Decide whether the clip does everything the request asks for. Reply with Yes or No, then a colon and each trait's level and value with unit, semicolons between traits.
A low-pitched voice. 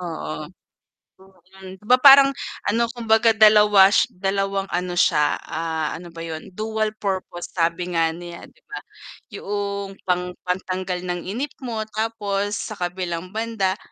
No: high, 190 Hz